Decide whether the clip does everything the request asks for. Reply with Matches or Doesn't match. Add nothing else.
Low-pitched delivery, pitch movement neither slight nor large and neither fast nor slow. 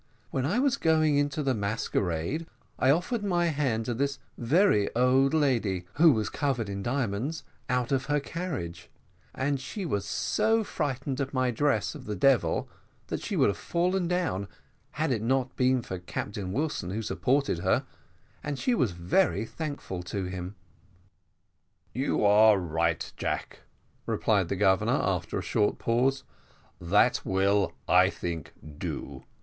Doesn't match